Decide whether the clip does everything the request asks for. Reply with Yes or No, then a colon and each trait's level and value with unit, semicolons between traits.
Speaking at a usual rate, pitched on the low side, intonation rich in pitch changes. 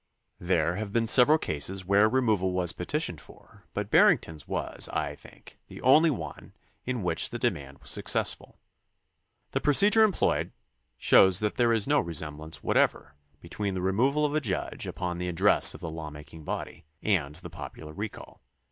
Yes: average, 165 wpm; very low, 95 Hz; wide, 6.5 semitones